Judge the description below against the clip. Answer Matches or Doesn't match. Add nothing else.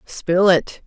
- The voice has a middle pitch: Matches